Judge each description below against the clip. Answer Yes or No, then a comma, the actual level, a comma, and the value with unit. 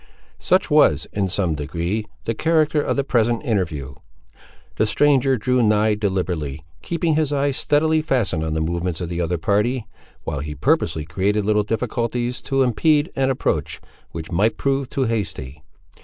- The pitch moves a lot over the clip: Yes, wide, 7.8 semitones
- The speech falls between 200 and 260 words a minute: No, average, 160 wpm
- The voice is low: Yes, low, 110 Hz